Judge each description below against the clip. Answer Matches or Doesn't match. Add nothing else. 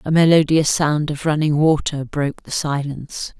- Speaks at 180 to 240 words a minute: Doesn't match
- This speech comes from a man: Doesn't match